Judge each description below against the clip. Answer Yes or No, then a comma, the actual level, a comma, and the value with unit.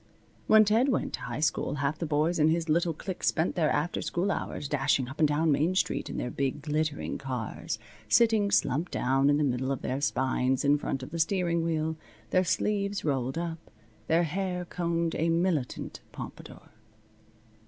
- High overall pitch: No, medium, 160 Hz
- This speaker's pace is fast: No, average, 185 wpm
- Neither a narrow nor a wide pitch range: Yes, average, 3.6 semitones